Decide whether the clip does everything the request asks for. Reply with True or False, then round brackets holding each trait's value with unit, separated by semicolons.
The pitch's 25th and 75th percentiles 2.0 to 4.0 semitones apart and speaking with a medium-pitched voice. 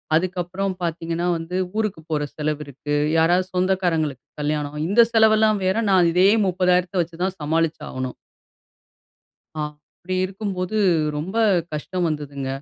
True (3.5 semitones; 175 Hz)